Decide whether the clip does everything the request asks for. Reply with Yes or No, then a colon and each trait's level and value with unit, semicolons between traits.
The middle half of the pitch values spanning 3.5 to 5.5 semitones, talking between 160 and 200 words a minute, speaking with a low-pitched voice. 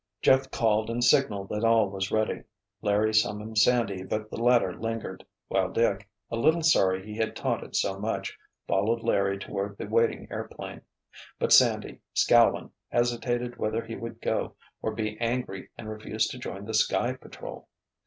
No: narrow, 2.4 semitones; average, 165 wpm; low, 110 Hz